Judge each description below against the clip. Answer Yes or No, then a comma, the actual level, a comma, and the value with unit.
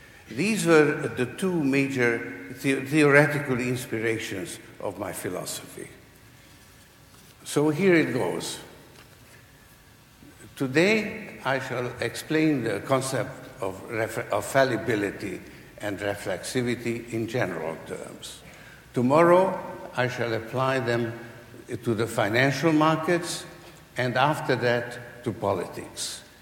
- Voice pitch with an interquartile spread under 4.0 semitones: No, average, 4.3 semitones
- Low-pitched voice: Yes, low, 125 Hz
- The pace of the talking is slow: Yes, slow, 100 wpm